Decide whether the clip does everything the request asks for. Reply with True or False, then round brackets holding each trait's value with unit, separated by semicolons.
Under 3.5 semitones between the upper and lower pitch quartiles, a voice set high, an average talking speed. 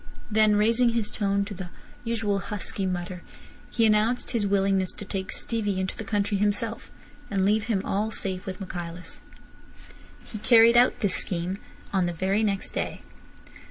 True (2.5 semitones; 200 Hz; 160 wpm)